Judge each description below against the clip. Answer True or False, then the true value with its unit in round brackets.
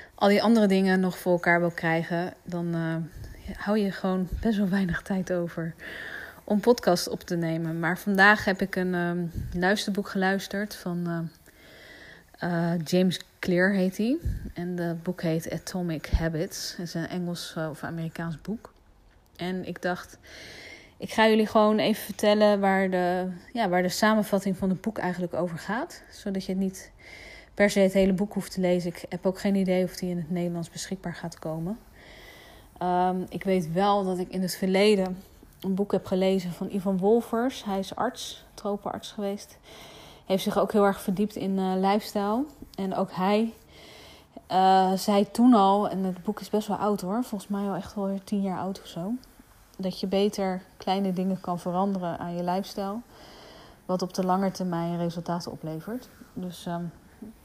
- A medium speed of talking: True (180 wpm)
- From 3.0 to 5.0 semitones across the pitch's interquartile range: False (2.4 semitones)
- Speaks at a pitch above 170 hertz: True (190 Hz)